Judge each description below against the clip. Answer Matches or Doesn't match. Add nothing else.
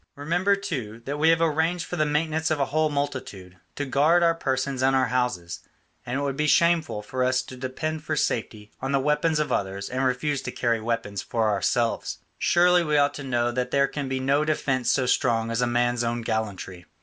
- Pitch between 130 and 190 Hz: Matches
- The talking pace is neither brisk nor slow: Doesn't match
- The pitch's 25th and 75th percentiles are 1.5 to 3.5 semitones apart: Doesn't match